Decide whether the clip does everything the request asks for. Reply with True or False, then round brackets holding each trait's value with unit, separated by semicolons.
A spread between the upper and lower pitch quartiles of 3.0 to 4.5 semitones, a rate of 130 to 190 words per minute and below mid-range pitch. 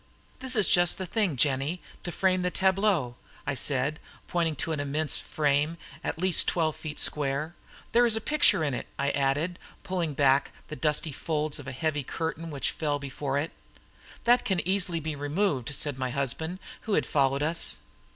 False (4.0 semitones; 180 wpm; 155 Hz)